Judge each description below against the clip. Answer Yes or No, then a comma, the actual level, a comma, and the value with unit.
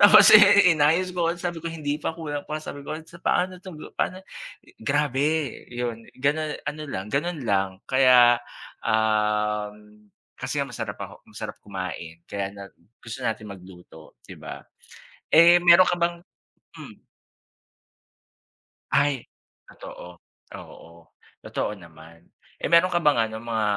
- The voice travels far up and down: Yes, wide, 8.0 semitones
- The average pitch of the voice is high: No, low, 135 Hz